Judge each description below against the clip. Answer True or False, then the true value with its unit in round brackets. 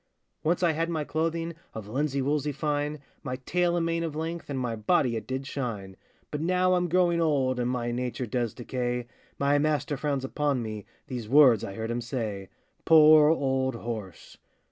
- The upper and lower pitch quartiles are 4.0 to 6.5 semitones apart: True (4.5 semitones)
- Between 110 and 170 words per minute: False (185 wpm)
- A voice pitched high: False (140 Hz)